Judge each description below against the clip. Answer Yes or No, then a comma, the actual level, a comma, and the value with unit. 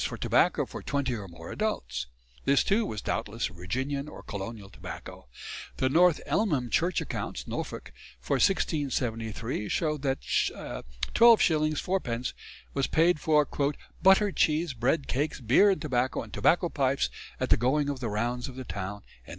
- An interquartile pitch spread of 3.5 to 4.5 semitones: No, wide, 5.6 semitones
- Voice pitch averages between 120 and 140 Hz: Yes, low, 135 Hz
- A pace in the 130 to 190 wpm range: Yes, average, 155 wpm